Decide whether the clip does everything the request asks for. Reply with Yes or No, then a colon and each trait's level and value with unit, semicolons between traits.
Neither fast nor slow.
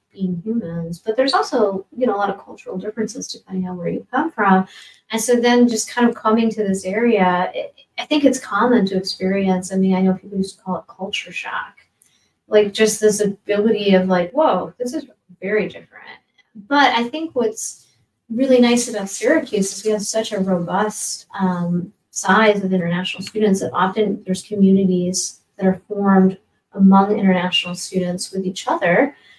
Yes: average, 180 wpm